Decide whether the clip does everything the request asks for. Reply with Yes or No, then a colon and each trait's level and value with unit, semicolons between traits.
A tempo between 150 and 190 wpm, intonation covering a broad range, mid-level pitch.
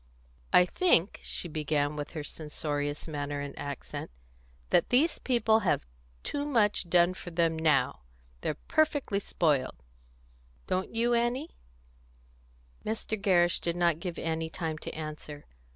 No: slow, 135 wpm; wide, 6.1 semitones; medium, 170 Hz